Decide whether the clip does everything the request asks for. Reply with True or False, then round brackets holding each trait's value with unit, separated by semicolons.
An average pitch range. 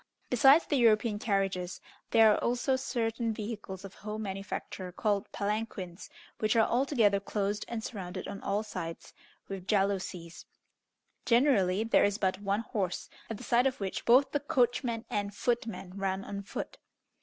True (3.1 semitones)